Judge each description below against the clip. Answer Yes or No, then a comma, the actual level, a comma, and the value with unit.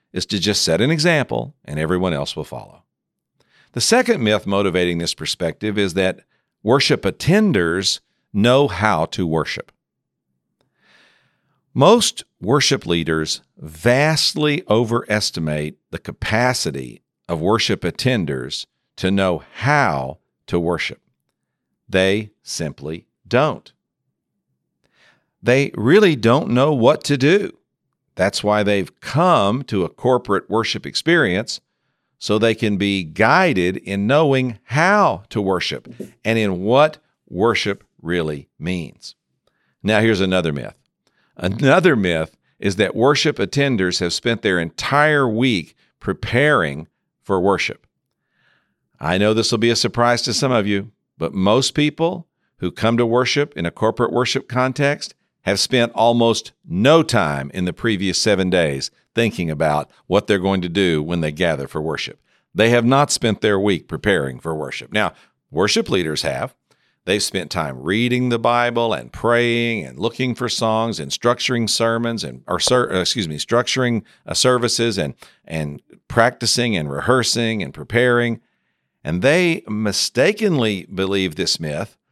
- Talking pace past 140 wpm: No, slow, 135 wpm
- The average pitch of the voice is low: Yes, low, 110 Hz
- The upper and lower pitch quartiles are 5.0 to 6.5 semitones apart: Yes, wide, 5.5 semitones